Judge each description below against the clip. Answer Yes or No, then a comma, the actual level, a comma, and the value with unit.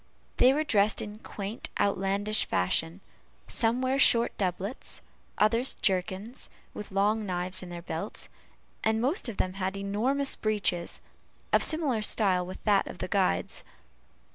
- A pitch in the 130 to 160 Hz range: No, high, 205 Hz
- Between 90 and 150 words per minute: Yes, average, 140 wpm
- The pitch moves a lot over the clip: No, average, 3.5 semitones